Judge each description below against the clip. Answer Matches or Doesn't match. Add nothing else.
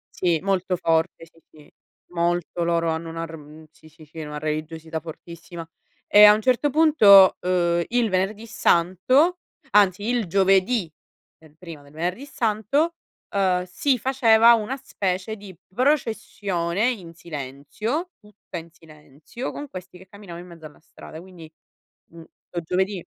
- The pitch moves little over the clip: Doesn't match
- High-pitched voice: Doesn't match